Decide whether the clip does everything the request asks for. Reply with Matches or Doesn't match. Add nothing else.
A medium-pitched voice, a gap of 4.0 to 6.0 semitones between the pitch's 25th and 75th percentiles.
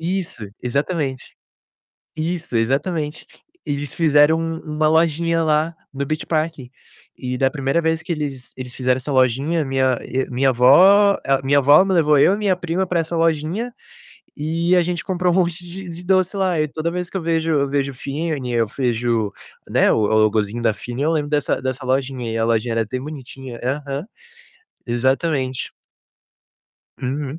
Matches